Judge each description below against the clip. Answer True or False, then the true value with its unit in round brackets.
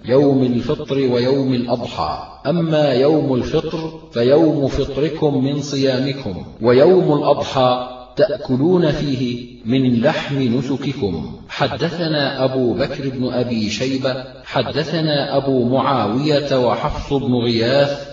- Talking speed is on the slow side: False (100 wpm)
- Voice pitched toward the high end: False (135 Hz)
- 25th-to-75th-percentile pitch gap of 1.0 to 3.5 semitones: True (2.5 semitones)